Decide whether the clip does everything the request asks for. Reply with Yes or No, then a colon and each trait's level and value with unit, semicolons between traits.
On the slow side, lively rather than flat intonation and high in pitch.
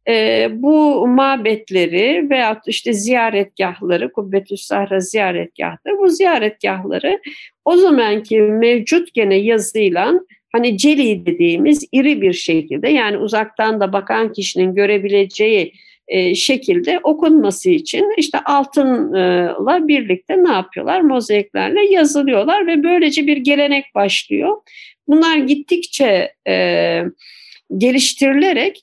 Yes: slow, 100 wpm; wide, 7.8 semitones; very high, 270 Hz